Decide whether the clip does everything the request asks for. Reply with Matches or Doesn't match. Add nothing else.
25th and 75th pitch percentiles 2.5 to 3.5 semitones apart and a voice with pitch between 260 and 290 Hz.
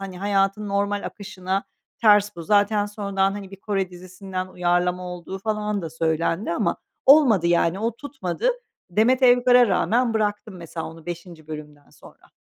Doesn't match